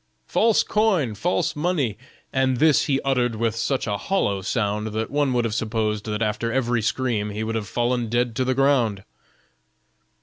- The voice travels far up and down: No, average, 3.8 semitones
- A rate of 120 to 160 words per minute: No, average, 175 wpm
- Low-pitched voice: Yes, low, 120 Hz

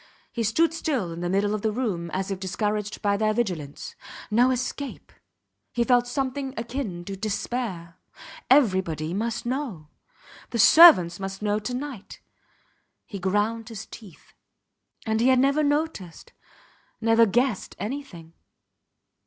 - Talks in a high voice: Yes, high, 220 Hz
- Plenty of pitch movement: No, average, 4.8 semitones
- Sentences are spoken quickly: No, slow, 135 wpm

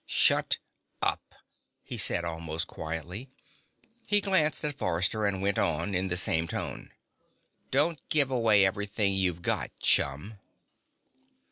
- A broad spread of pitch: Yes, wide, 6.1 semitones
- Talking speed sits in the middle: No, slow, 125 wpm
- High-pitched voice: No, very low, 95 Hz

